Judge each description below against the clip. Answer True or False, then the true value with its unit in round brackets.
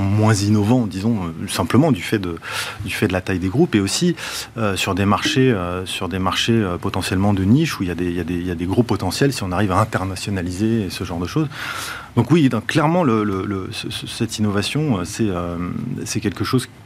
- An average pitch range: True (3.9 semitones)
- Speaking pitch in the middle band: False (105 Hz)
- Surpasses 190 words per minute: True (220 wpm)